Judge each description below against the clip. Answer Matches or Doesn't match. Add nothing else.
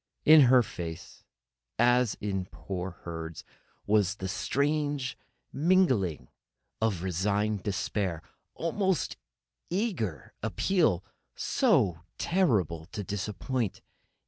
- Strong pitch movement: Matches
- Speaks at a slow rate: Matches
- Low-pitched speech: Matches